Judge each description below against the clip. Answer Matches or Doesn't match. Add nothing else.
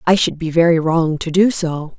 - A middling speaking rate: Doesn't match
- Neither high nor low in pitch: Matches